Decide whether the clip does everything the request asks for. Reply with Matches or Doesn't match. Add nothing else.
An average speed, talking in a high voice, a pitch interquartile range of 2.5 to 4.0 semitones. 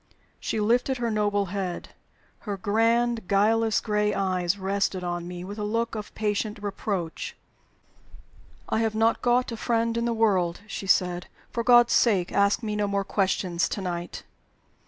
Matches